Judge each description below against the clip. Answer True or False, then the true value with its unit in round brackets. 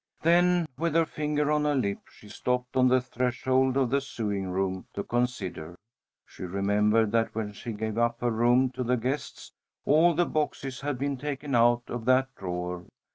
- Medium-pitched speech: False (125 Hz)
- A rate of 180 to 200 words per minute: True (185 wpm)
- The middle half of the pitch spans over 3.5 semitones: True (4.5 semitones)